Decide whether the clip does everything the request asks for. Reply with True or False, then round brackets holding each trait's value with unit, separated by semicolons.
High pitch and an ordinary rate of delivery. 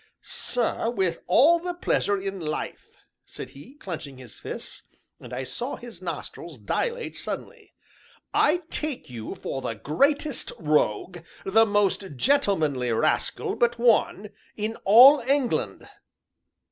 False (205 Hz; 125 wpm)